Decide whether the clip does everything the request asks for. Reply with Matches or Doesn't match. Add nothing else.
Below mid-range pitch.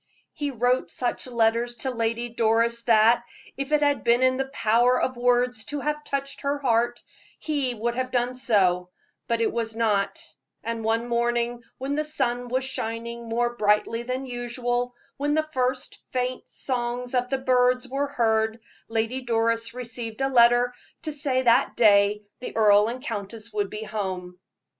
Doesn't match